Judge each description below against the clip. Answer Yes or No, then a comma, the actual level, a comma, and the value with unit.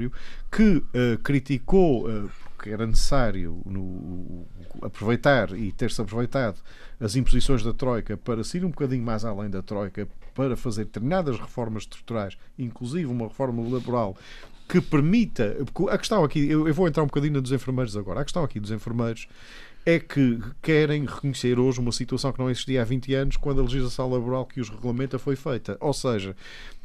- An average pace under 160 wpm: No, average, 170 wpm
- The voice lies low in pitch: Yes, low, 125 Hz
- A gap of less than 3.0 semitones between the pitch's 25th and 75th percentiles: No, average, 3.8 semitones